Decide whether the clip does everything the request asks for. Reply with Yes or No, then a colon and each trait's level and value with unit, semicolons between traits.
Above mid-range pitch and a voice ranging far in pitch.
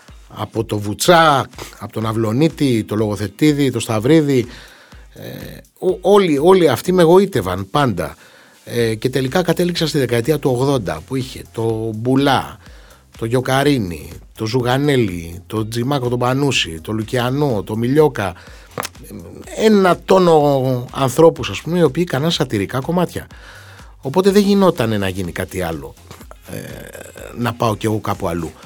No: low, 125 Hz; wide, 6.1 semitones